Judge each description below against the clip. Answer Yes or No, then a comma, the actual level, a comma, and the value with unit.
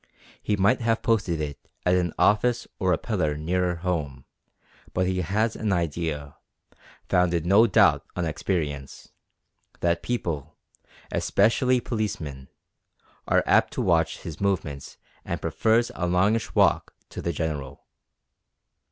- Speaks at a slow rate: Yes, slow, 130 wpm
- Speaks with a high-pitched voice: No, very low, 90 Hz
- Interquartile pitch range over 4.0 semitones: Yes, average, 5.1 semitones